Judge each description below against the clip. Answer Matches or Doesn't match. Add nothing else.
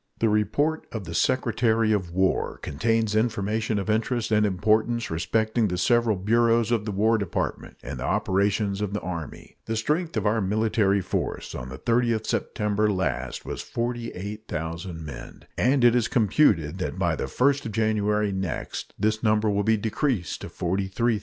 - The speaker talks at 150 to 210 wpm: Matches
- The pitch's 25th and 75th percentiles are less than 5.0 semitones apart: Matches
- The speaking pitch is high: Doesn't match